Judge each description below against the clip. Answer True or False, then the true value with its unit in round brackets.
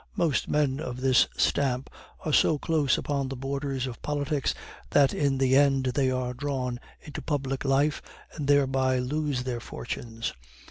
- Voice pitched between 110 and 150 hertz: True (135 Hz)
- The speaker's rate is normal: True (155 wpm)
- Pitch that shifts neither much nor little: False (1.9 semitones)